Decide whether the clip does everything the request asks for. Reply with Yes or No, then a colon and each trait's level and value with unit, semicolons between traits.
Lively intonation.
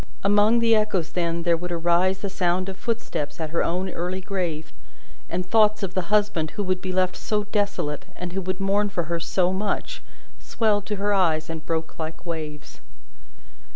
No: average, 3.3 semitones